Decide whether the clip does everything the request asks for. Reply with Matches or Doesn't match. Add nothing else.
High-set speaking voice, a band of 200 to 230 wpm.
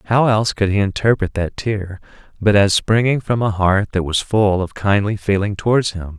Doesn't match